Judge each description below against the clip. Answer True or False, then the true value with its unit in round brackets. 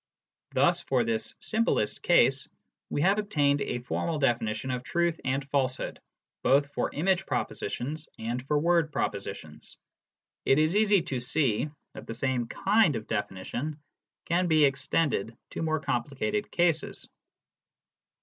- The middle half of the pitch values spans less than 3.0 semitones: False (5.2 semitones)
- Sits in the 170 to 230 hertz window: False (145 Hz)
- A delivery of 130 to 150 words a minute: True (140 wpm)